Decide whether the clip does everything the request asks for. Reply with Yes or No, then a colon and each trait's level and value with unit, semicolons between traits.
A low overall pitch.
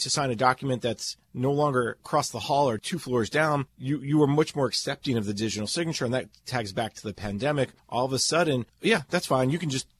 Yes: low, 130 Hz